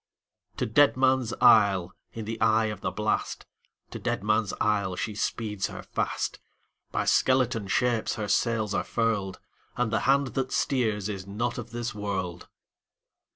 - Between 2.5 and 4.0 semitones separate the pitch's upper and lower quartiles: Yes, average, 2.8 semitones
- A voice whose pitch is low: Yes, low, 110 Hz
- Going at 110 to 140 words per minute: Yes, slow, 135 wpm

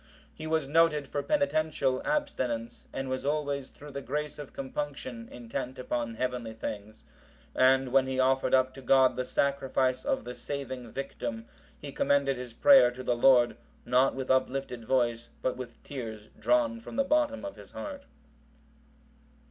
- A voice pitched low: Yes, low, 130 Hz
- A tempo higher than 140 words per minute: Yes, average, 160 wpm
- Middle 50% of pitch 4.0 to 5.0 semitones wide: No, average, 2.7 semitones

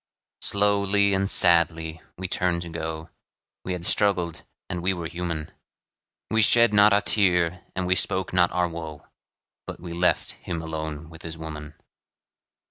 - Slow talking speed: No, average, 155 wpm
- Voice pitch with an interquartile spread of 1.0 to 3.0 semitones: Yes, average, 2.7 semitones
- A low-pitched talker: Yes, very low, 85 Hz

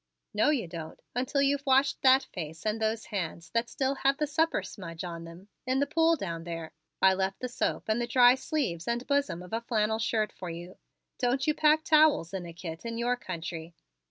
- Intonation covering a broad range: Yes, wide, 7.6 semitones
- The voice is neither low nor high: No, high, 225 Hz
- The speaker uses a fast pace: Yes, fast, 215 wpm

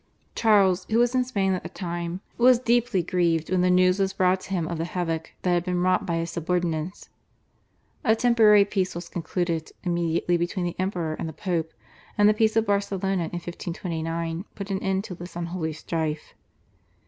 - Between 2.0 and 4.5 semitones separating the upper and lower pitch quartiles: Yes, average, 2.7 semitones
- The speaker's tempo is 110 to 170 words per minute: No, average, 190 wpm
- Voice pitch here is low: No, medium, 180 Hz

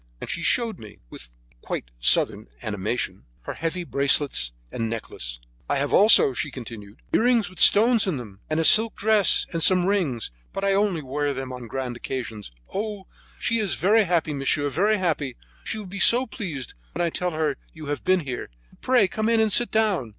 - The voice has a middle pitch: Yes, medium, 165 Hz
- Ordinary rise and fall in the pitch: No, wide, 8.0 semitones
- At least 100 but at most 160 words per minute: No, average, 195 wpm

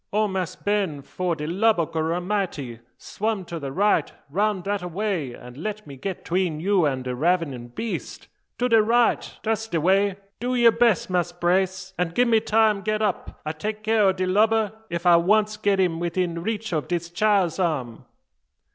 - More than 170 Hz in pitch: Yes, medium, 185 Hz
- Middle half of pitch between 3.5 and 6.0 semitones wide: Yes, average, 4.2 semitones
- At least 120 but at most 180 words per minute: No, average, 190 wpm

